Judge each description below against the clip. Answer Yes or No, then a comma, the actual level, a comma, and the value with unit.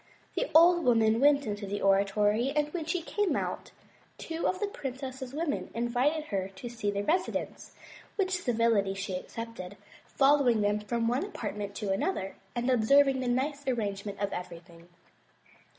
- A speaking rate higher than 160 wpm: No, average, 155 wpm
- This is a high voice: Yes, high, 240 Hz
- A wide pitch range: Yes, wide, 6.0 semitones